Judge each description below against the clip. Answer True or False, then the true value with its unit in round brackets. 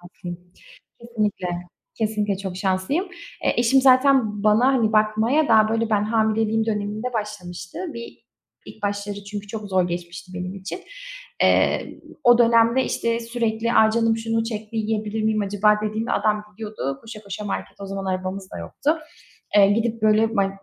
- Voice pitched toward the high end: True (215 Hz)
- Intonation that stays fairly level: True (2.1 semitones)